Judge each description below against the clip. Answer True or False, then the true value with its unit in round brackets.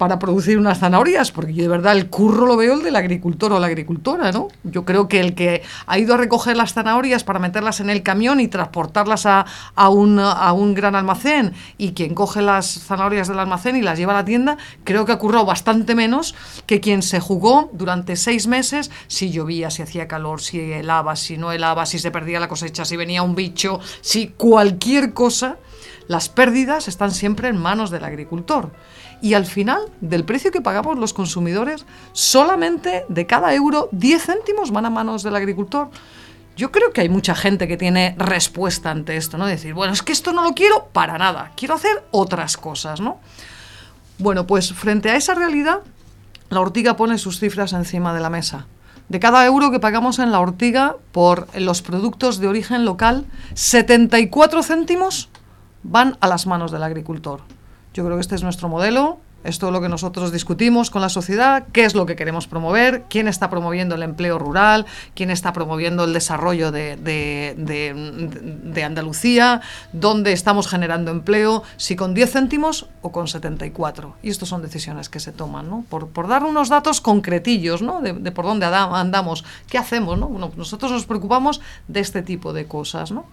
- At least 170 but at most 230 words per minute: True (190 wpm)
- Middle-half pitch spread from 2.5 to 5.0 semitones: False (5.4 semitones)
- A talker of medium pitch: False (195 Hz)